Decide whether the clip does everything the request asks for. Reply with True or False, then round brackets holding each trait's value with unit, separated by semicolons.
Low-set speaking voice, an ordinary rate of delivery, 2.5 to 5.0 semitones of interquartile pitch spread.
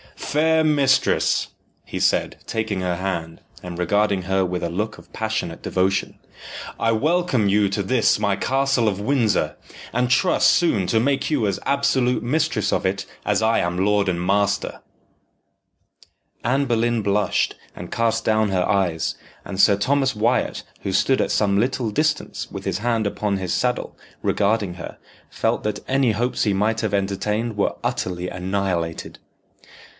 True (105 Hz; 160 wpm; 4.1 semitones)